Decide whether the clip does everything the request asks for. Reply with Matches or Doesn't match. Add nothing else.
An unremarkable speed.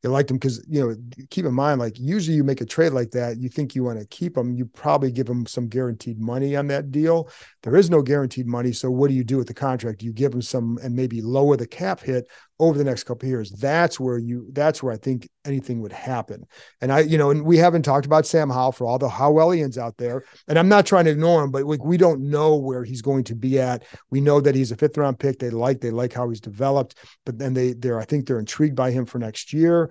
Doesn't match